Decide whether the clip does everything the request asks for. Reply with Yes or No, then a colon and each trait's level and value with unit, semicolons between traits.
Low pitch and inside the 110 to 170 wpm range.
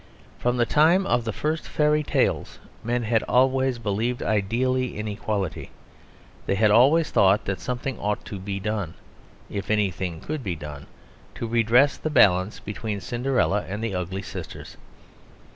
Yes: low, 110 Hz; average, 155 wpm